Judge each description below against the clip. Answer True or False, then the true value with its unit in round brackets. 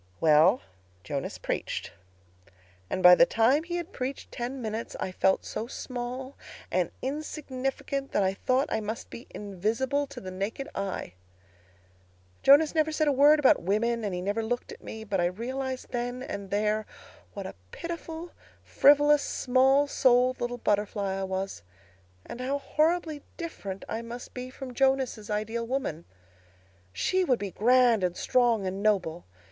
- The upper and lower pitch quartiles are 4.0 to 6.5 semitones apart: True (5.0 semitones)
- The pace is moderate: True (155 wpm)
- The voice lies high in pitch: True (245 Hz)